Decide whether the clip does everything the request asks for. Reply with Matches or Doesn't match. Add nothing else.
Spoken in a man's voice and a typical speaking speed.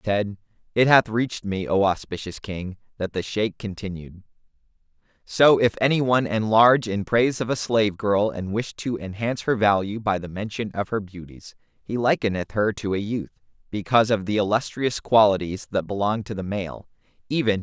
Matches